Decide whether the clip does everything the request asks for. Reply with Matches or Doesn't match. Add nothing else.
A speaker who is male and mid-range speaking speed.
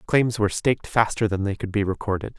Doesn't match